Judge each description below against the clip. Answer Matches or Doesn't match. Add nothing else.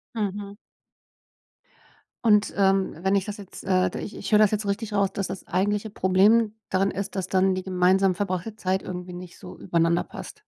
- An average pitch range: Doesn't match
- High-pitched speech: Matches